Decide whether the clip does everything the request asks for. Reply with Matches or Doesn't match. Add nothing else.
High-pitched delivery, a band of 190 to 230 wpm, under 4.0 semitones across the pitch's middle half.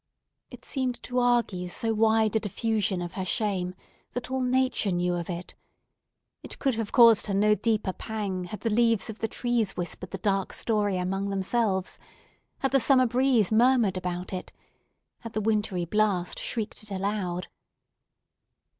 Doesn't match